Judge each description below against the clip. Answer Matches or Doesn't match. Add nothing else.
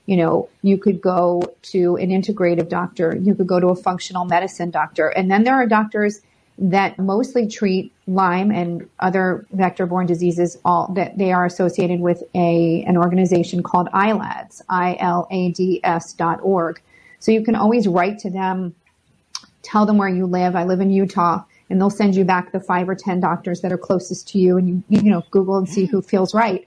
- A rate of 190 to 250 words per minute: Matches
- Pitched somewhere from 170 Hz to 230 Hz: Matches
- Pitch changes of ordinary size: Doesn't match